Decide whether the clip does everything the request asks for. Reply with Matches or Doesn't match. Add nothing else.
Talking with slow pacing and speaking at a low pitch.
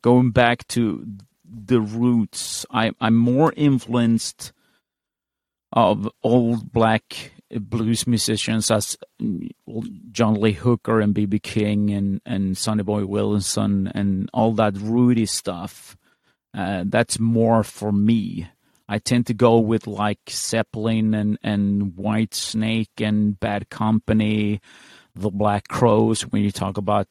Matches